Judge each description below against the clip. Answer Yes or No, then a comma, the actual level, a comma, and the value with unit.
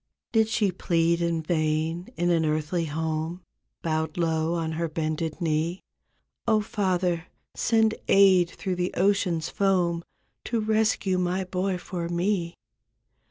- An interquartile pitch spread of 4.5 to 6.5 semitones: No, average, 2.7 semitones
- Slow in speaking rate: Yes, slow, 130 wpm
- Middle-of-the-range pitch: Yes, medium, 175 Hz